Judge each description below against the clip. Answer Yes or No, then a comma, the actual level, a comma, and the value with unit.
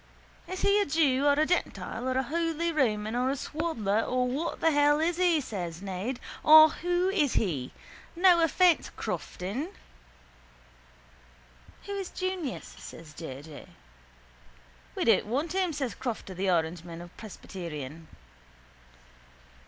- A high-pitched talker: Yes, very high, 265 Hz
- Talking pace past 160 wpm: No, slow, 135 wpm